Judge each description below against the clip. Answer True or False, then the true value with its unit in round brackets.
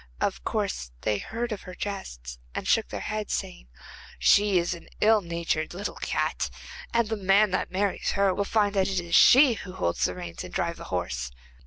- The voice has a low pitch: False (190 Hz)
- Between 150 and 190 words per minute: False (205 wpm)